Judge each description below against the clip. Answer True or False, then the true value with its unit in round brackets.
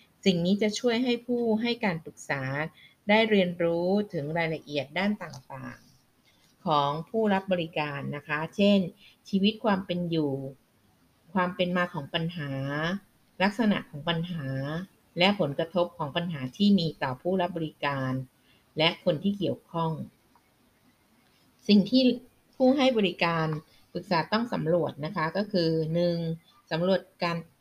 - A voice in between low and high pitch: True (170 Hz)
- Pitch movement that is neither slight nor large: True (4.8 semitones)